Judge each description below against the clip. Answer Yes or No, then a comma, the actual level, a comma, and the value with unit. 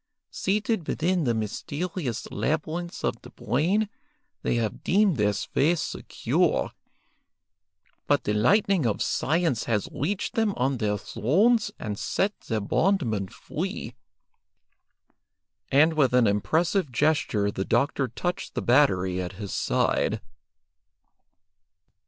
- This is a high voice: No, medium, 140 Hz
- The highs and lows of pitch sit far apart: Yes, wide, 8.4 semitones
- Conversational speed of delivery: No, slow, 115 wpm